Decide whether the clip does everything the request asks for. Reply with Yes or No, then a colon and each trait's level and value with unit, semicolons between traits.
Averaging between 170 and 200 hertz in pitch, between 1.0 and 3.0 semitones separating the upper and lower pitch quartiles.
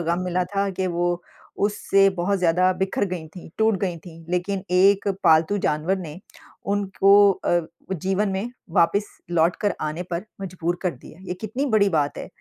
Yes: medium, 185 Hz; narrow, 2.6 semitones